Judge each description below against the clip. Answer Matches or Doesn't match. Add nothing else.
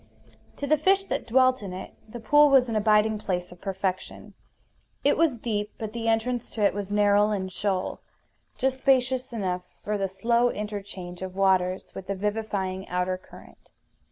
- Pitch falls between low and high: Doesn't match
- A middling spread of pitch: Matches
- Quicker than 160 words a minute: Matches